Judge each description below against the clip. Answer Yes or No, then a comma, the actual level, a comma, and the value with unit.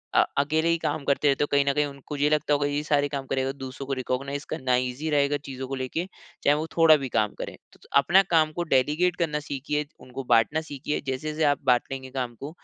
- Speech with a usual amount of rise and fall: No, narrow, 2.3 semitones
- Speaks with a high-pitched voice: No, medium, 140 Hz